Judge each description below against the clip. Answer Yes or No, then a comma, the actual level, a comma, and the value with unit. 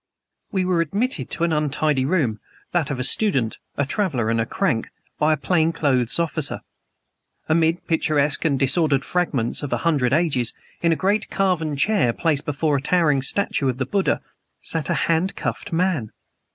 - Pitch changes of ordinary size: Yes, average, 4.3 semitones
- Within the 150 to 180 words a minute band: Yes, average, 175 wpm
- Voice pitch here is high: No, medium, 155 Hz